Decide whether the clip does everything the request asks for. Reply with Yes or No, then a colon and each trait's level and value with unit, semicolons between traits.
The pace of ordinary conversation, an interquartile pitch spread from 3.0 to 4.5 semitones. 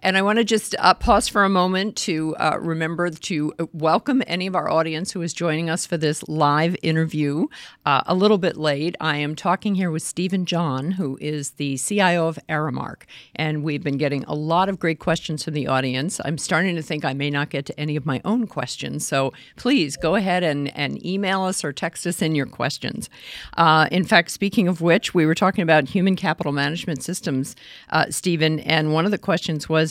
No: fast, 215 wpm; average, 3.3 semitones